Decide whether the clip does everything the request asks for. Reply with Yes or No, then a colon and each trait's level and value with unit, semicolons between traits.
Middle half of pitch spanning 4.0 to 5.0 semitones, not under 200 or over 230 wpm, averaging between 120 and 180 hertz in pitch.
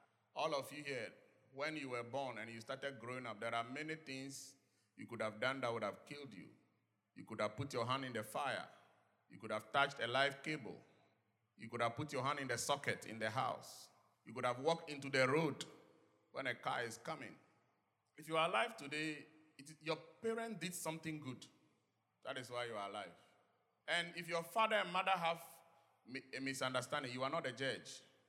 Yes: average, 4.3 semitones; fast, 205 wpm; low, 135 Hz